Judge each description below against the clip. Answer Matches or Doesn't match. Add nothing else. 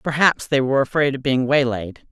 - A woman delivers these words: Matches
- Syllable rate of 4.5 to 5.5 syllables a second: Matches